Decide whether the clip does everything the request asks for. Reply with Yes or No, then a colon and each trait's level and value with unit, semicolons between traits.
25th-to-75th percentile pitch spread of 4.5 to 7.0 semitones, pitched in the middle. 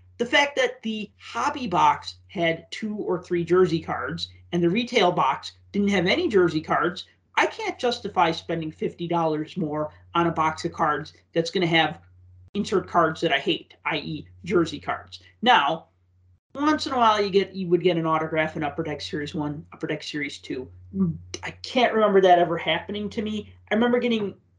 Yes: wide, 5.4 semitones; medium, 170 Hz